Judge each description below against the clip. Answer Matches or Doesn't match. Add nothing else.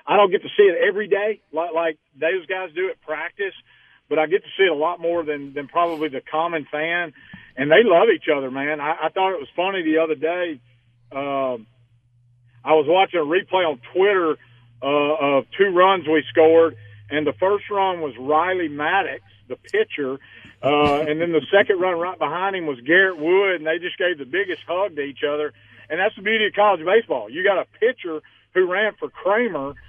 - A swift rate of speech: Matches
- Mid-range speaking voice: Matches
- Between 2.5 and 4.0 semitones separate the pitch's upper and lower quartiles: Doesn't match